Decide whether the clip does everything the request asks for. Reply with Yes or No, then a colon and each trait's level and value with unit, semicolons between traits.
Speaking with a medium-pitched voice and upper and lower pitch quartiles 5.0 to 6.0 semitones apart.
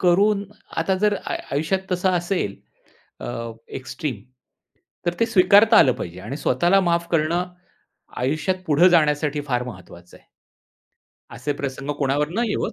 Yes: medium, 155 Hz; average, 5.3 semitones